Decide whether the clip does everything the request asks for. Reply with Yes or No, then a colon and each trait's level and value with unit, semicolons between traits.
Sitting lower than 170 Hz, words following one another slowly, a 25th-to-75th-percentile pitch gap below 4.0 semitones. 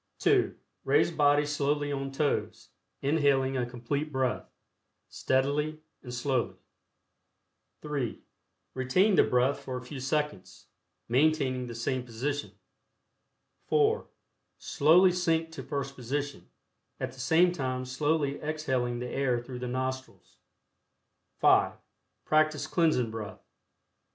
Yes: medium, 140 Hz; slow, 115 wpm; average, 3.2 semitones